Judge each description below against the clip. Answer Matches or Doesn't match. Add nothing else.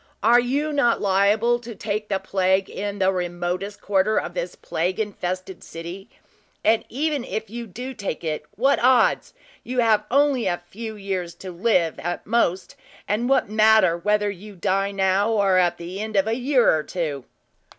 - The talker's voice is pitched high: Matches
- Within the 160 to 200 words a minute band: Matches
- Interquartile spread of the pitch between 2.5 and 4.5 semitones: Matches